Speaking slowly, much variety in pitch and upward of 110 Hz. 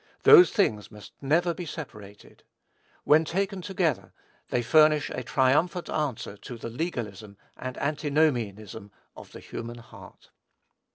Yes: slow, 125 wpm; wide, 6.3 semitones; low, 135 Hz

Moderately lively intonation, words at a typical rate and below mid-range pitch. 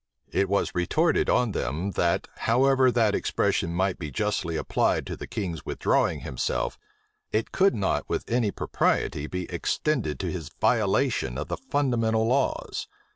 No: wide, 6.6 semitones; average, 150 wpm; low, 100 Hz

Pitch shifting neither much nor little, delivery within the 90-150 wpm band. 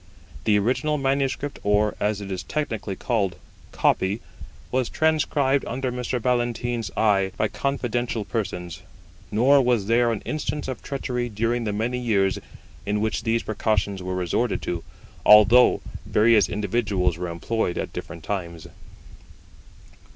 Yes: average, 3.8 semitones; slow, 135 wpm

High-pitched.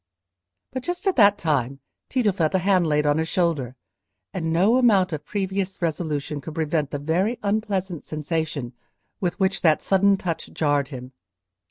No: medium, 170 Hz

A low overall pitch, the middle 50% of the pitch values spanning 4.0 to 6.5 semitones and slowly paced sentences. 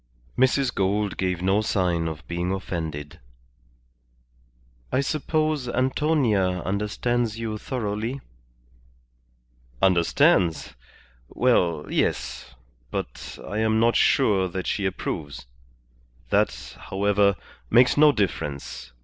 Yes: low, 100 Hz; average, 5.0 semitones; slow, 95 wpm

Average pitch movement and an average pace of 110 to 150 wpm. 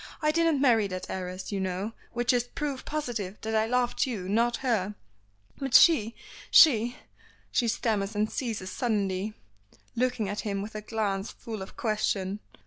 No: average, 3.5 semitones; average, 165 wpm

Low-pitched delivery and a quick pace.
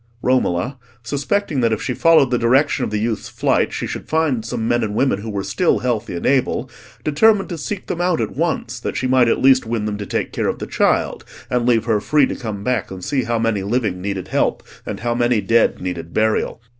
Yes: low, 120 Hz; fast, 230 wpm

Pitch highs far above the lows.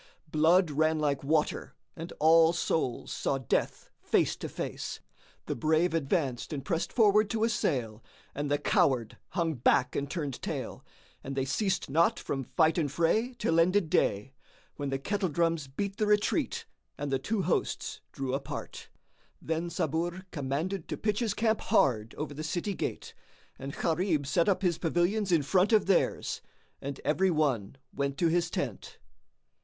No: average, 4.8 semitones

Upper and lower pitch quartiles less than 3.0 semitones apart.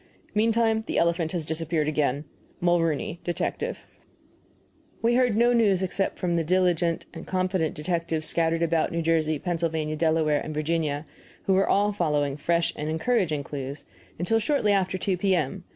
No: average, 3.4 semitones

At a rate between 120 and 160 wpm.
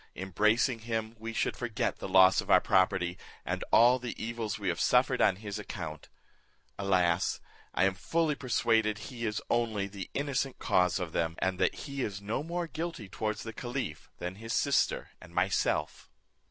No: average, 175 wpm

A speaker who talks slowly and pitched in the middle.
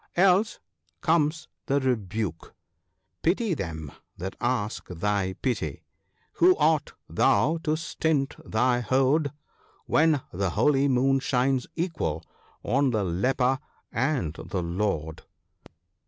No: slow, 115 wpm; low, 130 Hz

